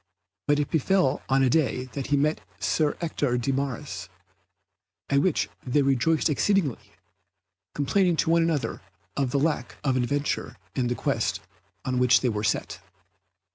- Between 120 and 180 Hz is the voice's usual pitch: Yes, medium, 140 Hz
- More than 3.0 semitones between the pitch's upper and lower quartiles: Yes, average, 3.7 semitones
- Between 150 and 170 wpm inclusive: Yes, average, 155 wpm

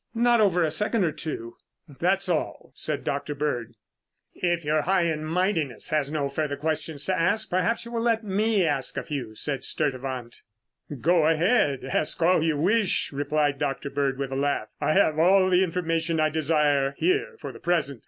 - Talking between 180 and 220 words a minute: Yes, average, 185 wpm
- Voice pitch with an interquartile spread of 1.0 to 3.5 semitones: No, average, 4.4 semitones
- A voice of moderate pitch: Yes, medium, 155 Hz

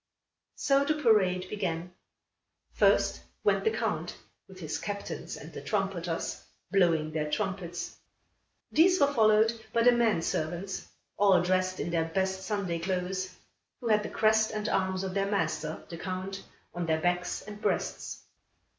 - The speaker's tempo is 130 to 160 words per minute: Yes, average, 150 wpm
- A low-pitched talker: No, high, 190 Hz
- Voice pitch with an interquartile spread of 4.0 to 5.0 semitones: No, average, 3.3 semitones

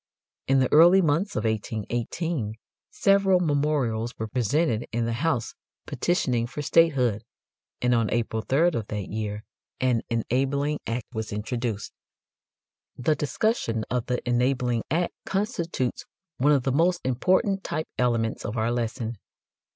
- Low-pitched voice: Yes, low, 125 Hz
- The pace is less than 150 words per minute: Yes, slow, 135 wpm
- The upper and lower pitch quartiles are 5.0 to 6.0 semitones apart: Yes, average, 5.3 semitones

